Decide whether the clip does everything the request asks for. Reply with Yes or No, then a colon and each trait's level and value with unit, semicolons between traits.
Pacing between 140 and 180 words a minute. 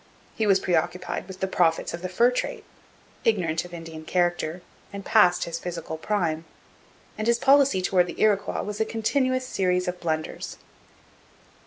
Yes: average, 160 wpm